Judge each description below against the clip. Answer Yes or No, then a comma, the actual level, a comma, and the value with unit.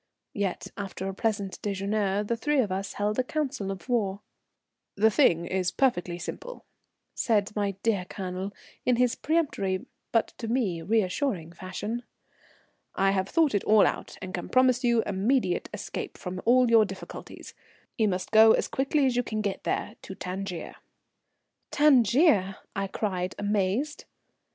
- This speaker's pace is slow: No, average, 155 wpm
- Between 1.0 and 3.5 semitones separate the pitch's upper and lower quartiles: No, average, 4.2 semitones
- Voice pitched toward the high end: Yes, high, 205 Hz